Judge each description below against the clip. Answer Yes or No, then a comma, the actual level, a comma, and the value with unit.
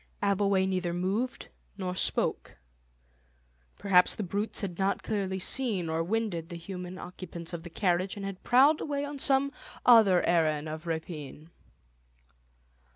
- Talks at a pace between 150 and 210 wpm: No, average, 140 wpm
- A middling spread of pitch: Yes, average, 3.3 semitones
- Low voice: No, medium, 185 Hz